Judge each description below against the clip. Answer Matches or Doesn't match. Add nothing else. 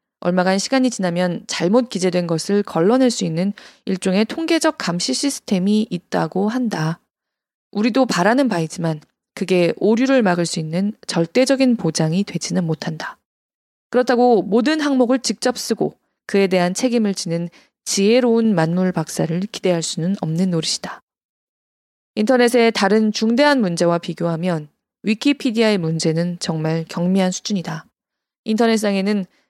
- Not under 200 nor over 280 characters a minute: Doesn't match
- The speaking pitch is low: Doesn't match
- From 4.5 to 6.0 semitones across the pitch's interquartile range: Matches